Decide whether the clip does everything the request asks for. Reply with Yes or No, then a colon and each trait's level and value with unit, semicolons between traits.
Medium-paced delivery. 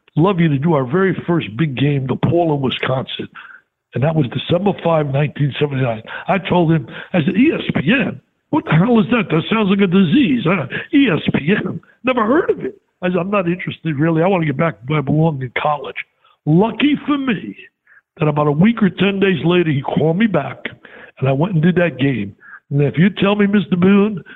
No: fast, 215 wpm